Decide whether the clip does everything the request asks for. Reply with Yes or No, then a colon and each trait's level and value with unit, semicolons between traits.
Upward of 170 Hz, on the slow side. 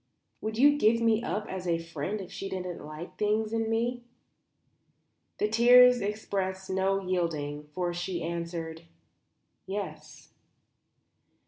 Yes: high, 190 Hz; slow, 125 wpm